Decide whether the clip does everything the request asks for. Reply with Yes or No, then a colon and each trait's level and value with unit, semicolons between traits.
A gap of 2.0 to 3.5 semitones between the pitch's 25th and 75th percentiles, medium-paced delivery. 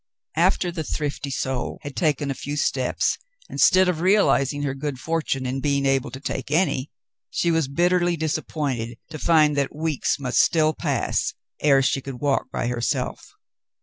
Yes: average, 3.2 semitones; average, 165 wpm